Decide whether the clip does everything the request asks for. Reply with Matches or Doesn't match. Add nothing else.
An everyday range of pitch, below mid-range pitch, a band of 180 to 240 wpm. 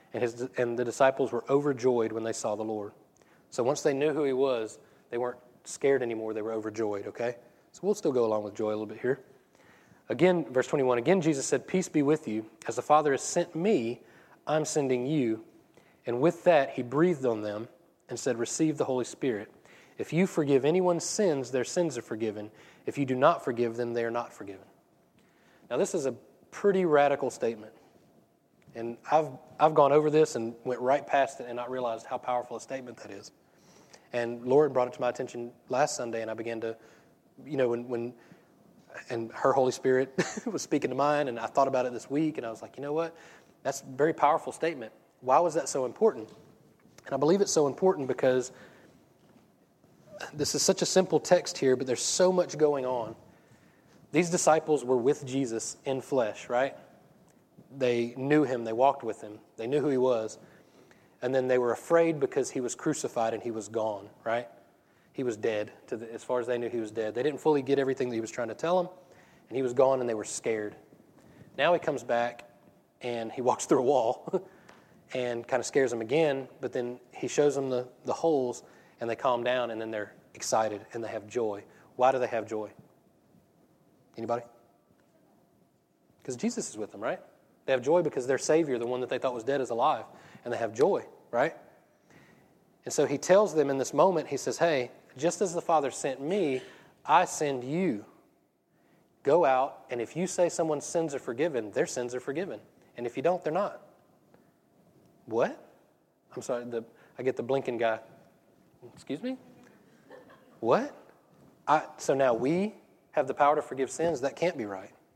Matches